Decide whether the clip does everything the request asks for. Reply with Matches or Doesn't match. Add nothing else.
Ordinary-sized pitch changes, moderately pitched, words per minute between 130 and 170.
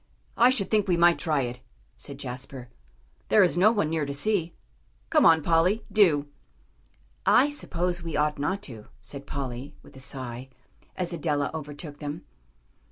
Matches